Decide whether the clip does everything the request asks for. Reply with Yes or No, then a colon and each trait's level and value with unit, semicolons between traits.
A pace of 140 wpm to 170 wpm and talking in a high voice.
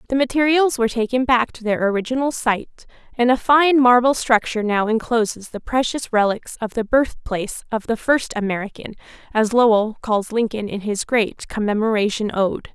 Yes: average, 165 wpm; high, 230 Hz